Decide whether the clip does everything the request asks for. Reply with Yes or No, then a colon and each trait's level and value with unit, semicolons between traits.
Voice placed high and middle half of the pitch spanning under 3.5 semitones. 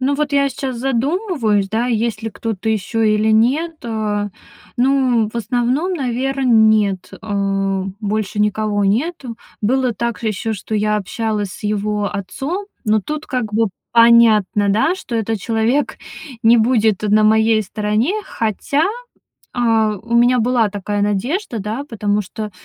Yes: high, 220 Hz; average, 3.0 semitones